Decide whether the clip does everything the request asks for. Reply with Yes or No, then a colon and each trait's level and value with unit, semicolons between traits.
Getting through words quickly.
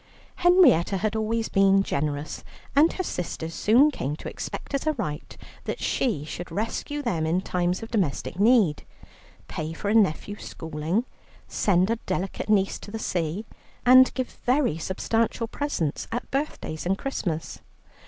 No: average, 155 wpm